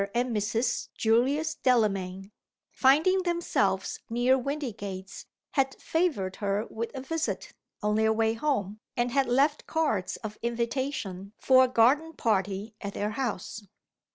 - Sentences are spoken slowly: Yes, slow, 130 wpm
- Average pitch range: Yes, average, 4.7 semitones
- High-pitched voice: Yes, high, 235 Hz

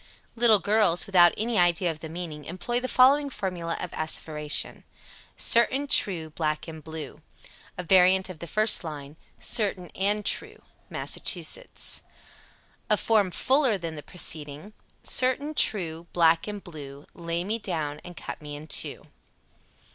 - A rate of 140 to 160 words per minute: Yes, average, 150 wpm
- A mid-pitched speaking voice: Yes, medium, 175 Hz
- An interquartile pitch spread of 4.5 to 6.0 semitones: Yes, average, 5.0 semitones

